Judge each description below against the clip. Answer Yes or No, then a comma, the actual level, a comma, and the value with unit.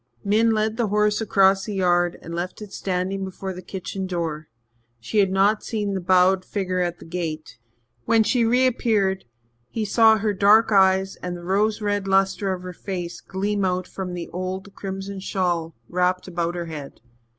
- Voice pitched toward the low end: No, high, 190 Hz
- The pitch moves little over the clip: Yes, narrow, 2.3 semitones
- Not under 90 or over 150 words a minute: No, average, 185 wpm